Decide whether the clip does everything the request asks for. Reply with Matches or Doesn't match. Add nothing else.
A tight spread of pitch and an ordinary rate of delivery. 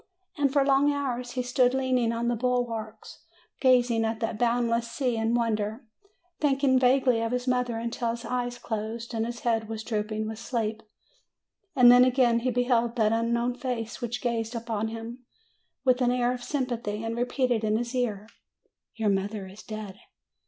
Matches